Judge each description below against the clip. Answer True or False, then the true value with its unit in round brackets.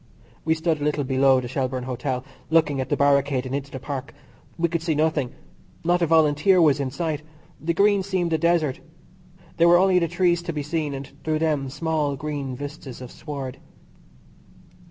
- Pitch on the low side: False (150 Hz)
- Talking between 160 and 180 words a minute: False (190 wpm)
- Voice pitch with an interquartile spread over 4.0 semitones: False (3.4 semitones)